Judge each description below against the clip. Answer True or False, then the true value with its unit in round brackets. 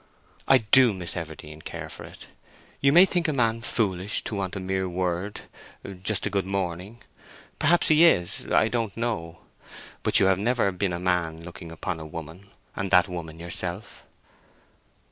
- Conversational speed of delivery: True (165 wpm)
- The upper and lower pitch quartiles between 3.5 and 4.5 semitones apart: True (4.1 semitones)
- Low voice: True (95 Hz)